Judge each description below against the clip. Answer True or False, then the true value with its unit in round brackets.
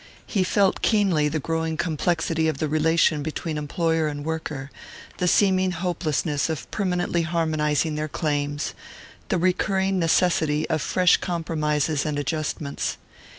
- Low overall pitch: False (160 Hz)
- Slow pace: True (130 wpm)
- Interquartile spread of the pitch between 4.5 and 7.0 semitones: False (2.7 semitones)